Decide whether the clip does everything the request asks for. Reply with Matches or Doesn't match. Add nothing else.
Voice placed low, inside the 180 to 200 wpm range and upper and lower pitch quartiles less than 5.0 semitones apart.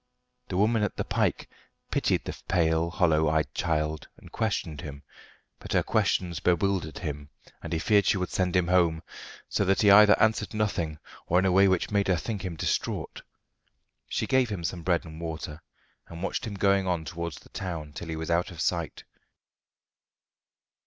Matches